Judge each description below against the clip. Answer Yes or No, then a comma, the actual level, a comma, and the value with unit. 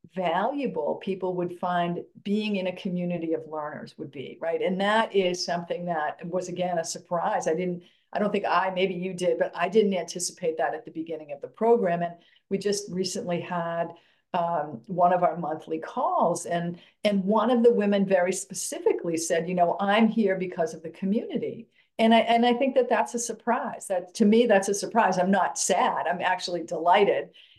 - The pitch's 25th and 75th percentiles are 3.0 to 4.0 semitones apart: Yes, average, 3.4 semitones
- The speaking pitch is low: No, medium, 185 Hz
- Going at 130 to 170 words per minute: No, average, 200 wpm